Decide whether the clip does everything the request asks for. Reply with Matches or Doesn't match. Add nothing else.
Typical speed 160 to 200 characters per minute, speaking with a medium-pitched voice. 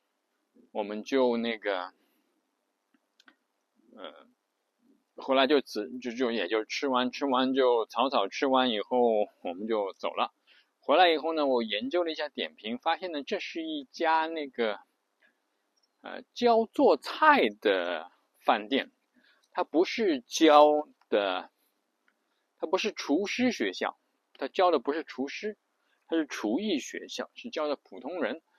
Matches